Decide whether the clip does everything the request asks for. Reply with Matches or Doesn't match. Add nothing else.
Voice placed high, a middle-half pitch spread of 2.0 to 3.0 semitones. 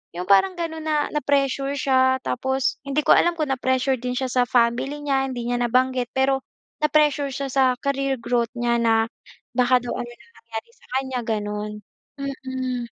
Matches